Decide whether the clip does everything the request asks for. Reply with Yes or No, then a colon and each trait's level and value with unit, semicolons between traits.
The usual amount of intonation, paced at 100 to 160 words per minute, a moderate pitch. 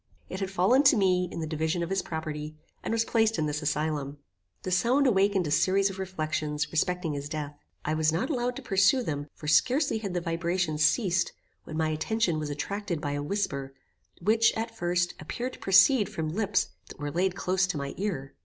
No: average, 4.6 semitones; fast, 205 wpm; medium, 175 Hz